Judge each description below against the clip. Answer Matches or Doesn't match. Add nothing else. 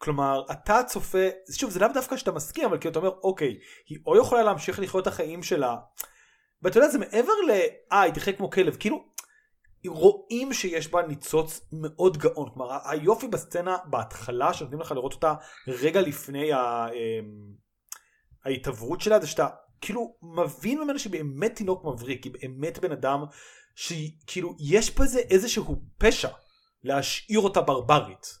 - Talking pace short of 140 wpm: Doesn't match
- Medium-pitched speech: Matches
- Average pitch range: Doesn't match